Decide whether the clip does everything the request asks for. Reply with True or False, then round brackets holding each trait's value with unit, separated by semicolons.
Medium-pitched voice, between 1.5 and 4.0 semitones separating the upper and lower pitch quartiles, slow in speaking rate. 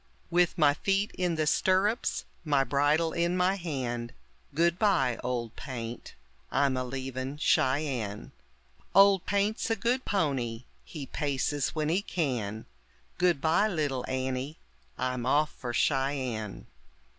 False (145 Hz; 5.4 semitones; 120 wpm)